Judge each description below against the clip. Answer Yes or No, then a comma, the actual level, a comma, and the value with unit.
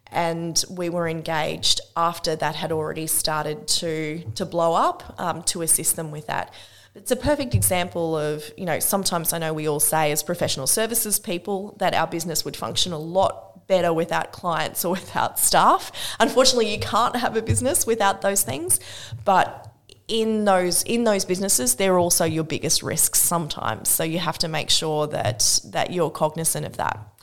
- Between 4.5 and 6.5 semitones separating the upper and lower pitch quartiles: No, average, 3.6 semitones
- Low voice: No, medium, 170 Hz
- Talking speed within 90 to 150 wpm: No, average, 180 wpm